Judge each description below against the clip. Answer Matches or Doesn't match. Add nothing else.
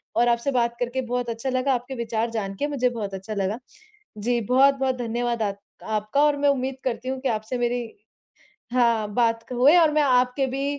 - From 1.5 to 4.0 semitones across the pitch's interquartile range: Matches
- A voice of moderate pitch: Doesn't match